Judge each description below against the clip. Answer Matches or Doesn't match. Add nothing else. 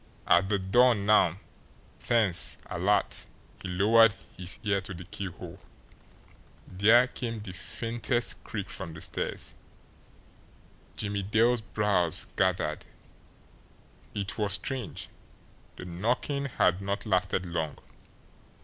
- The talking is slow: Matches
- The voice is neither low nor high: Doesn't match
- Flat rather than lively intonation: Doesn't match